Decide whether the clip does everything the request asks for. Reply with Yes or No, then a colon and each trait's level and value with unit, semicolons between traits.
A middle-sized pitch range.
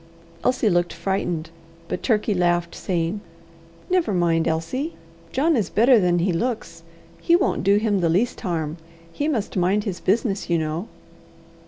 Yes: average, 5.0 semitones